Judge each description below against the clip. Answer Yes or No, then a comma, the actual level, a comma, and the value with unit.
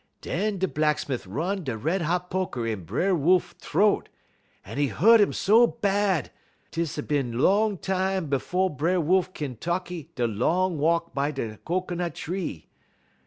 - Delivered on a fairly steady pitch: No, average, 4.7 semitones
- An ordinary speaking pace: Yes, average, 160 wpm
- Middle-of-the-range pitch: Yes, medium, 170 Hz